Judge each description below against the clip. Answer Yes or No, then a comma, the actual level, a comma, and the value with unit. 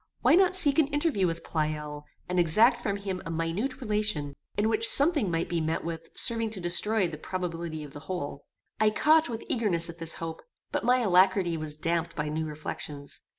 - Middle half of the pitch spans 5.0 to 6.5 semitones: Yes, wide, 5.6 semitones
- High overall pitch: No, medium, 180 Hz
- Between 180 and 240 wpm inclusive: Yes, average, 195 wpm